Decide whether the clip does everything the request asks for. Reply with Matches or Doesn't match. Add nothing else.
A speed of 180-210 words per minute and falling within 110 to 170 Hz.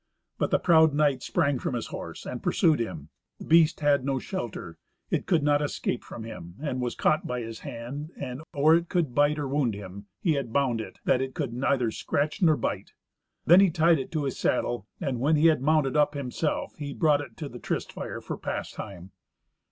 Matches